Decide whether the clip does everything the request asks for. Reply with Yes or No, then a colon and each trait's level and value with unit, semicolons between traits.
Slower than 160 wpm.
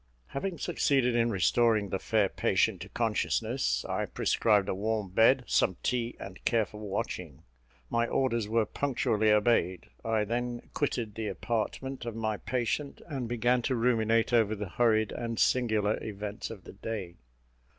Yes: average, 150 wpm